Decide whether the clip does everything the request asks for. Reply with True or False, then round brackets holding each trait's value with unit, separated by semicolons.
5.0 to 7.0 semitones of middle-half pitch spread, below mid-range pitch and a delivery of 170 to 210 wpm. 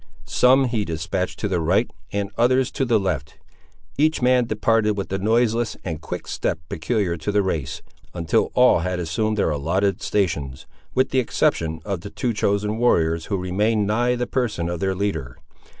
True (5.4 semitones; 100 Hz; 175 wpm)